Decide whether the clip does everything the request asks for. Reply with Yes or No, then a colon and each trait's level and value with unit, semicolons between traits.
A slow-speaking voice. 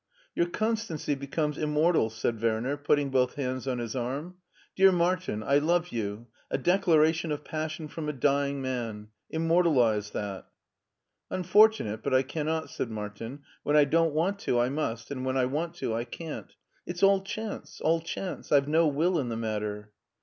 No: average, 185 wpm